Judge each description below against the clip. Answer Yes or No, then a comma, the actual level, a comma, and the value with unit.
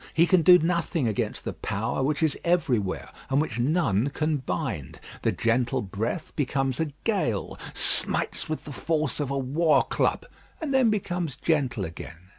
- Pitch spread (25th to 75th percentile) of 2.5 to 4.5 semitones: No, wide, 5.6 semitones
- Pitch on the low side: No, medium, 145 Hz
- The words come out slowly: No, average, 165 wpm